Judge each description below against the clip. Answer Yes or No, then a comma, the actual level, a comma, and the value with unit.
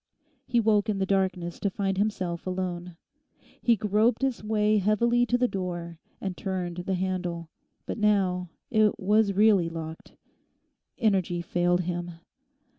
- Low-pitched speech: No, high, 190 Hz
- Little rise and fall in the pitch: No, average, 3.2 semitones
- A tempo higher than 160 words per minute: No, average, 140 wpm